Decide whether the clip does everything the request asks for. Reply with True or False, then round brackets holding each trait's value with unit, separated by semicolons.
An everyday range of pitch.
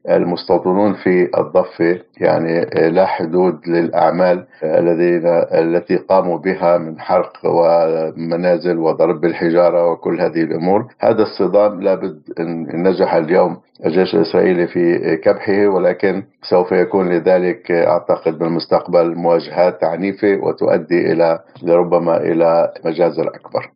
False (1.6 semitones)